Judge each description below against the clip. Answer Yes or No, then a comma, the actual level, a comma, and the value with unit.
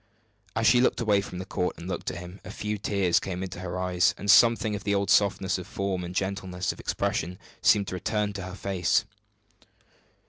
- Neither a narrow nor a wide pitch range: No, narrow, 1.9 semitones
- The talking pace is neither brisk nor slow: No, fast, 210 wpm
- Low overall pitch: Yes, very low, 95 Hz